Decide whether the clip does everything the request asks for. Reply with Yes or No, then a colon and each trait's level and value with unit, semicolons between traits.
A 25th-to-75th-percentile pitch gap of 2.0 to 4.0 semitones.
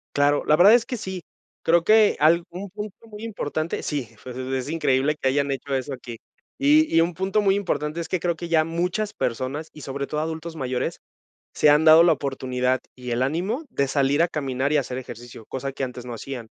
No: average, 4.8 semitones